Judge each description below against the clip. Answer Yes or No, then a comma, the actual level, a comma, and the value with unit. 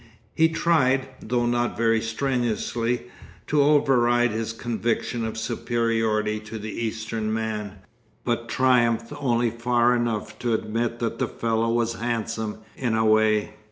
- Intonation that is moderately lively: No, narrow, 1.5 semitones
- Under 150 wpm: Yes, slow, 135 wpm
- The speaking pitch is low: Yes, low, 115 Hz